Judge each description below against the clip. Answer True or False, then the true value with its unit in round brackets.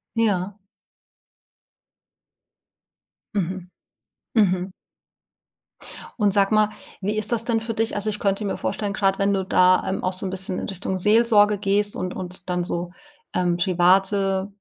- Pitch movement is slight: True (2.1 semitones)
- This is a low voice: False (195 Hz)